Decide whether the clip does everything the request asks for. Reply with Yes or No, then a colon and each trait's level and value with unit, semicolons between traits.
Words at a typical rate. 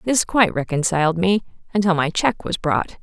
Yes: average, 180 wpm